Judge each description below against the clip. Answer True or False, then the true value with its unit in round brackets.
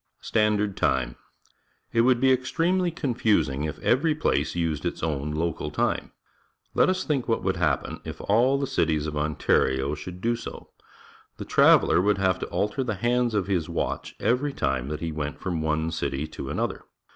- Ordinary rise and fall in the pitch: False (8.0 semitones)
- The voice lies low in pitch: True (95 Hz)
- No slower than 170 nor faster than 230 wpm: True (180 wpm)